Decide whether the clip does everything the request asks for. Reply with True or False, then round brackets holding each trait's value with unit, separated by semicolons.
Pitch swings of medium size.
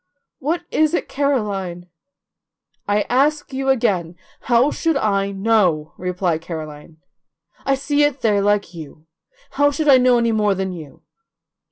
False (7.2 semitones)